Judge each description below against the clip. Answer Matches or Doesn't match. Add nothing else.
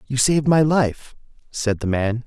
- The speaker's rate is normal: Matches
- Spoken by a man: Matches